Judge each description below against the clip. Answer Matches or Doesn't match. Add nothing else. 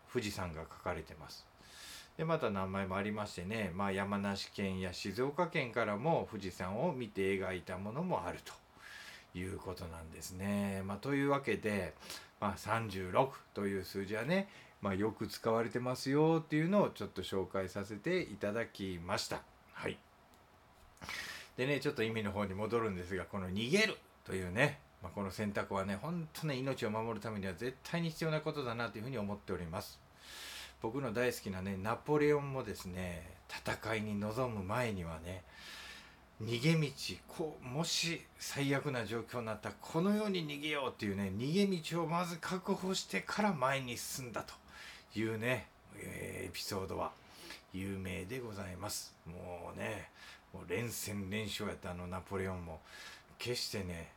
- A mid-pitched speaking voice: Doesn't match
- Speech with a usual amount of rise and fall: Doesn't match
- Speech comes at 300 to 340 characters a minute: Matches